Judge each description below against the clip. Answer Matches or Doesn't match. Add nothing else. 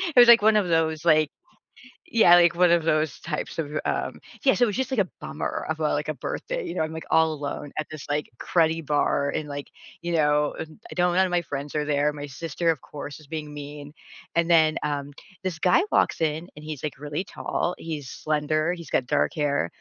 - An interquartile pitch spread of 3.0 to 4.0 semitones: Doesn't match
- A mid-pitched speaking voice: Matches